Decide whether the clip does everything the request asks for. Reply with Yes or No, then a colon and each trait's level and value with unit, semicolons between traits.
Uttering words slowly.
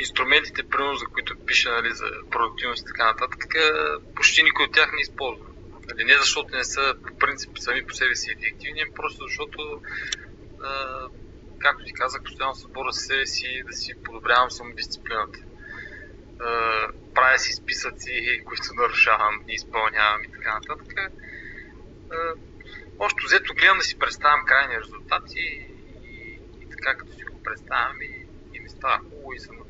No: average, 155 wpm